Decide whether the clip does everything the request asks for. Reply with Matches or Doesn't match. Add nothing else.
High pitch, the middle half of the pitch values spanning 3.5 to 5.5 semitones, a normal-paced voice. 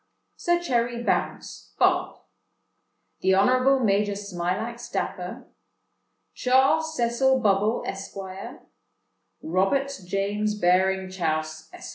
Doesn't match